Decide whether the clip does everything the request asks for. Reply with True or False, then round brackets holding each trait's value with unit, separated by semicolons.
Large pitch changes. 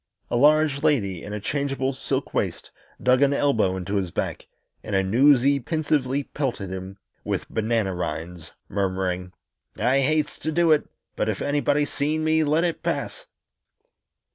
True (7.1 semitones)